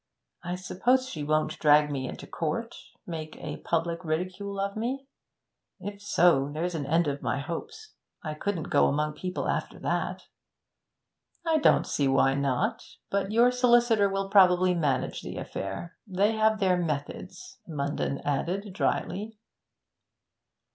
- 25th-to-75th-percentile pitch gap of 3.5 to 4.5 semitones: No, average, 5.1 semitones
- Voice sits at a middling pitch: Yes, medium, 180 Hz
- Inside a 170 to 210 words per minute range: No, average, 140 wpm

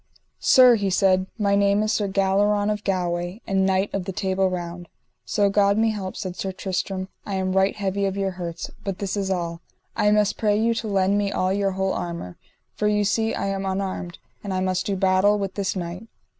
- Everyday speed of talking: No, fast, 215 wpm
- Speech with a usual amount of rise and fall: No, narrow, 1.5 semitones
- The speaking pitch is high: Yes, high, 195 Hz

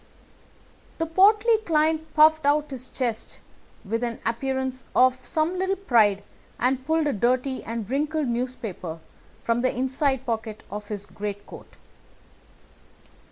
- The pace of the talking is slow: Yes, slow, 125 wpm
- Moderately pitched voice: No, very high, 260 Hz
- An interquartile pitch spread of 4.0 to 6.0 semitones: Yes, average, 5.2 semitones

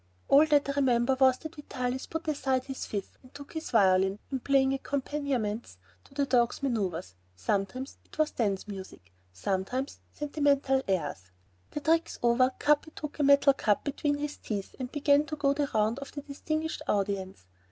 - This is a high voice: Yes, very high, 265 Hz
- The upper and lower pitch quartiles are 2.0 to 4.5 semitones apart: No, wide, 5.4 semitones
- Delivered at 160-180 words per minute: Yes, average, 175 wpm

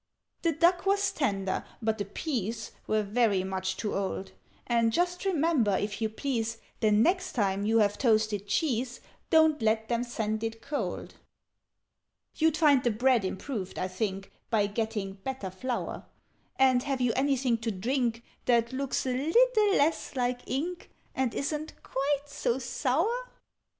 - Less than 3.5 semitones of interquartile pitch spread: No, average, 4.8 semitones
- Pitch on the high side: Yes, high, 240 Hz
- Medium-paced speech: Yes, average, 150 wpm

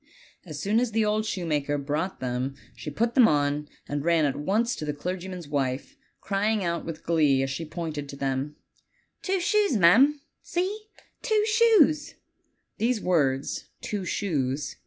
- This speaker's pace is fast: No, average, 155 wpm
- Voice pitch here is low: No, medium, 170 Hz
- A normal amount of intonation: No, wide, 7.6 semitones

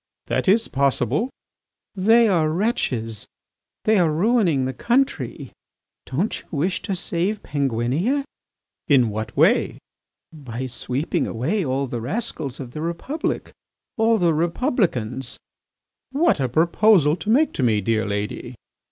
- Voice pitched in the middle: Yes, medium, 155 Hz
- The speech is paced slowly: Yes, slow, 130 wpm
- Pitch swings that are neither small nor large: No, wide, 9.0 semitones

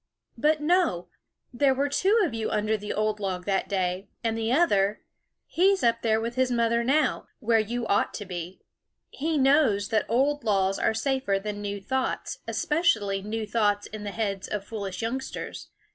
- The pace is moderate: Yes, average, 185 wpm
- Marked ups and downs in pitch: No, average, 4.5 semitones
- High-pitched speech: Yes, high, 225 Hz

